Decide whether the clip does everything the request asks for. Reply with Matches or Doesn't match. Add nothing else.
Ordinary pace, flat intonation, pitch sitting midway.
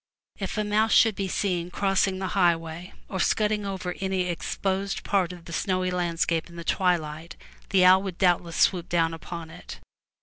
Matches